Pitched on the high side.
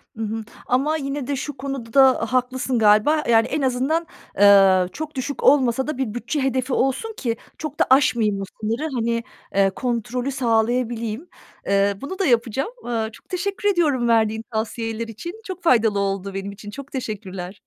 Yes: high, 240 Hz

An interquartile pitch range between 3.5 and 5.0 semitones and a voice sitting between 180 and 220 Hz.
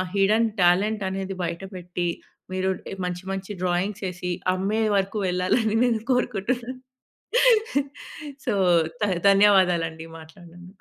No: average, 2.9 semitones; high, 190 Hz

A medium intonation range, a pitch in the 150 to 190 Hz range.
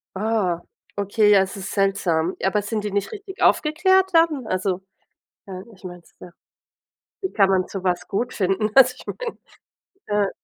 No: average, 5.0 semitones; high, 200 Hz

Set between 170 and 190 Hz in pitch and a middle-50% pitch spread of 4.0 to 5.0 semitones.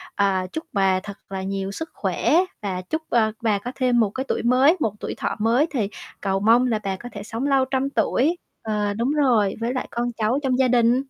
No: high, 230 Hz; average, 4.3 semitones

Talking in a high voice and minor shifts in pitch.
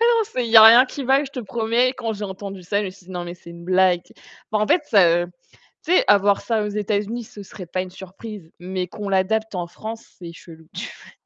No: high, 205 Hz; average, 3.6 semitones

